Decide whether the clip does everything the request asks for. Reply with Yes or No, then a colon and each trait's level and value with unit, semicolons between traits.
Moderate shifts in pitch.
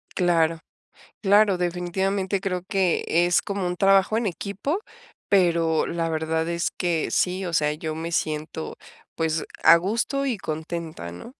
Yes: average, 3.2 semitones